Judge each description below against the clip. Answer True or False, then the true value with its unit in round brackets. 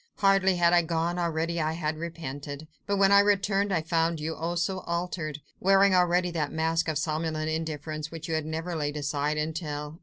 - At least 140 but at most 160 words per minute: False (190 wpm)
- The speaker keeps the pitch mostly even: True (2.3 semitones)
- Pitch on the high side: False (165 Hz)